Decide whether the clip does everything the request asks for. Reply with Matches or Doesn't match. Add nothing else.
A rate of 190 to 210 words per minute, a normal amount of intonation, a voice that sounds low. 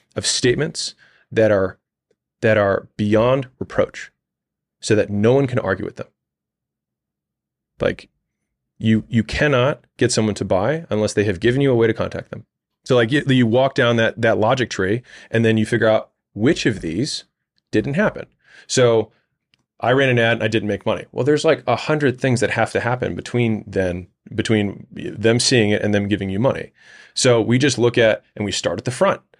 Matches